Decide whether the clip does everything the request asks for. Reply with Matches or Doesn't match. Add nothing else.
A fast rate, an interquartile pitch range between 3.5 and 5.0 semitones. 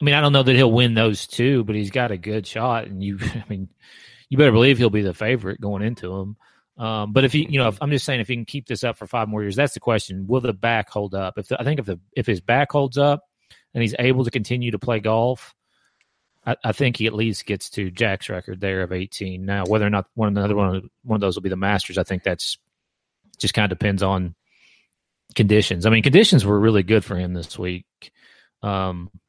Matches